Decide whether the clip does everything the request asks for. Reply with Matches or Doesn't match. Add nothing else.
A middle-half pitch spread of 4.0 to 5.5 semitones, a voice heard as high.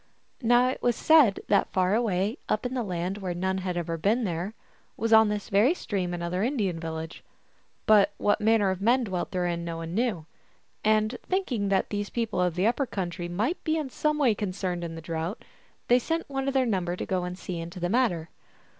Matches